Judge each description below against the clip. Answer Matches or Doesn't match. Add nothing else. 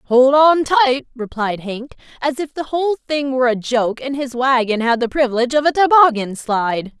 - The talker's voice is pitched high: Matches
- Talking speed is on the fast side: Doesn't match